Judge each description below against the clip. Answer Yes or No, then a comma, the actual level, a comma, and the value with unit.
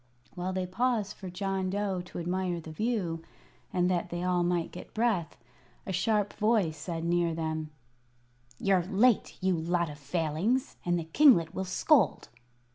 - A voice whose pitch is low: No, medium, 180 Hz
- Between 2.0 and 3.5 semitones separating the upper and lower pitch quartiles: Yes, average, 2.9 semitones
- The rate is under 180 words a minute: Yes, average, 160 wpm